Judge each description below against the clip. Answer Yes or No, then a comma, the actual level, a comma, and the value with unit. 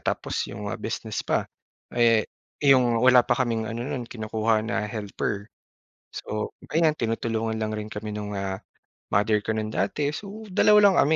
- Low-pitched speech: Yes, low, 110 Hz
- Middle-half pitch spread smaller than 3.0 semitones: Yes, narrow, 2.5 semitones